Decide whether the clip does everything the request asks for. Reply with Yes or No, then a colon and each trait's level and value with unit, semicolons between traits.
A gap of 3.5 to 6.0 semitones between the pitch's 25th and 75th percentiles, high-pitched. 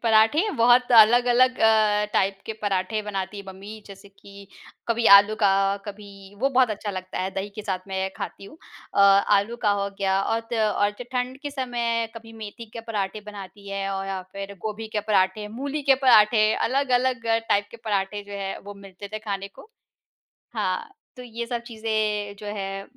No: average, 2.8 semitones; high, 210 Hz